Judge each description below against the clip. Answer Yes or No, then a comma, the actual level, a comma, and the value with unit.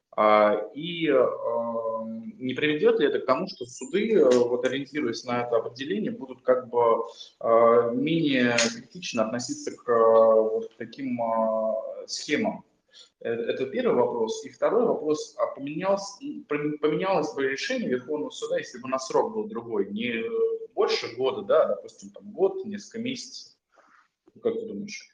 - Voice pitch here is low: No, medium, 165 Hz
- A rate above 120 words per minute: Yes, average, 130 wpm